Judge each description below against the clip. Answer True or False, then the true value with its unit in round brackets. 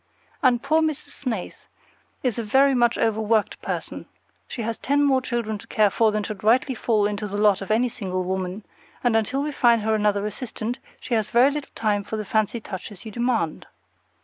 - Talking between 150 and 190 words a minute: False (200 wpm)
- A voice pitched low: False (220 Hz)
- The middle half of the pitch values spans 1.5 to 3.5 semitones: True (3.0 semitones)